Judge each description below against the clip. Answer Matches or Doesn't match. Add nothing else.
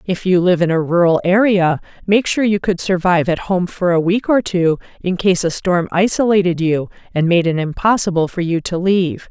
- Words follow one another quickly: Matches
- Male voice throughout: Doesn't match